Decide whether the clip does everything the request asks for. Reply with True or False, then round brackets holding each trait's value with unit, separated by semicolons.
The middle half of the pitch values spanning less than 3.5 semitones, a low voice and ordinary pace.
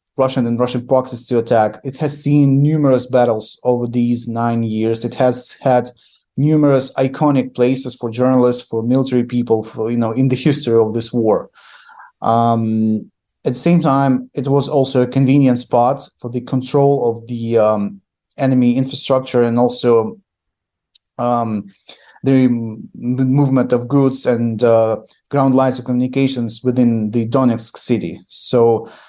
True (2.4 semitones; 125 Hz; 155 wpm)